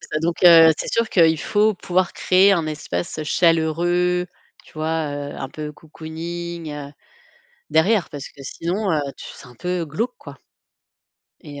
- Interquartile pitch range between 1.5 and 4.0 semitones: Yes, average, 2.8 semitones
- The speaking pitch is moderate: Yes, medium, 165 Hz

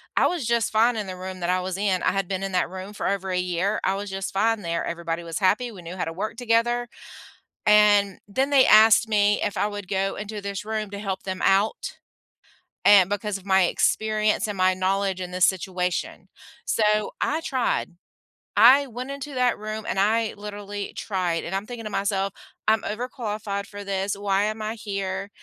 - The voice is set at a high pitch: Yes, high, 205 Hz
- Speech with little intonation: Yes, narrow, 2.3 semitones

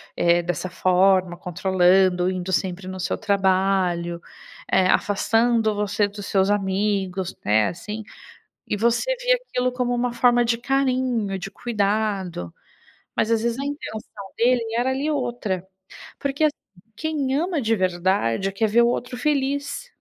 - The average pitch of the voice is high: Yes, high, 210 Hz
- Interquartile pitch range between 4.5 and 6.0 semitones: Yes, average, 4.8 semitones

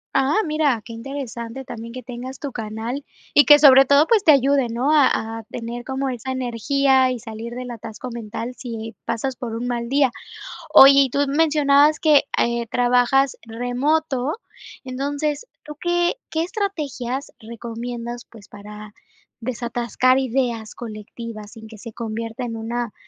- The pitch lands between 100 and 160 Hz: No, very high, 250 Hz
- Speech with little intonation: No, average, 3.2 semitones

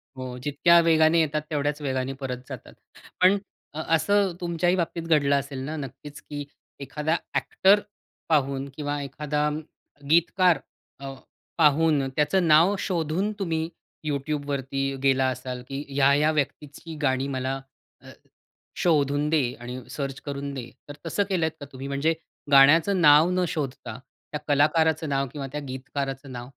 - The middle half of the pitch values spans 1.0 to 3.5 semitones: Yes, average, 2.9 semitones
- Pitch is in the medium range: Yes, medium, 145 Hz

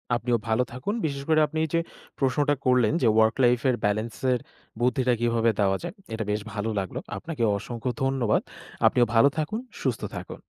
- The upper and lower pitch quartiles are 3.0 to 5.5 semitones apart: Yes, average, 3.3 semitones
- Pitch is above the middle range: No, low, 125 Hz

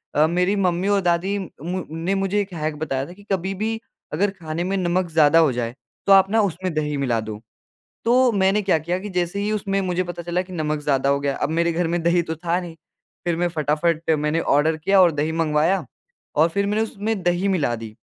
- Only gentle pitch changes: No, average, 3.7 semitones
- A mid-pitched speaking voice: Yes, medium, 175 Hz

